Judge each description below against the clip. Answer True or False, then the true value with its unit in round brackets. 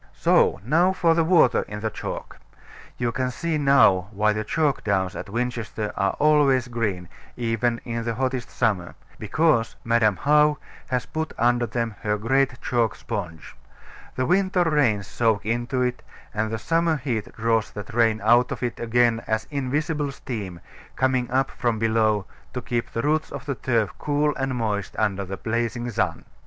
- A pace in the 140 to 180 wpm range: True (170 wpm)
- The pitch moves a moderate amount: True (4.0 semitones)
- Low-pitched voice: True (120 Hz)